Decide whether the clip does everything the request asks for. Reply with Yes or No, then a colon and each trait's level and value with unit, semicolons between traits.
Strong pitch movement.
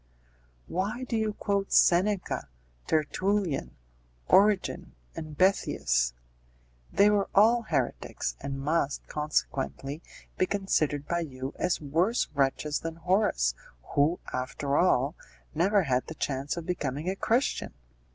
Yes: wide, 5.9 semitones